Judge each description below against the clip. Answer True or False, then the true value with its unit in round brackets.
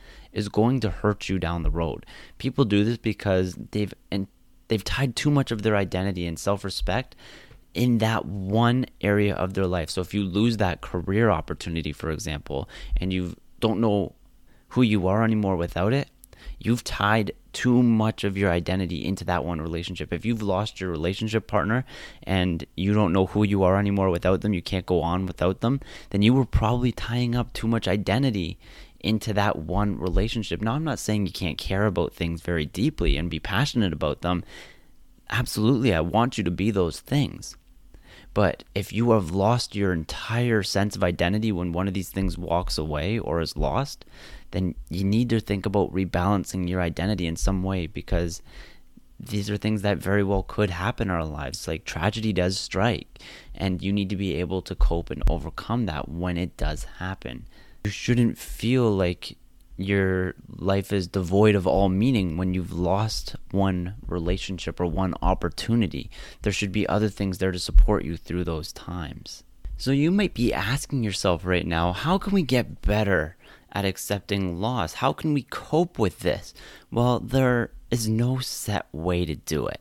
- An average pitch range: True (3.8 semitones)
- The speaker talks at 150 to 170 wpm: False (185 wpm)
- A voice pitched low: True (95 Hz)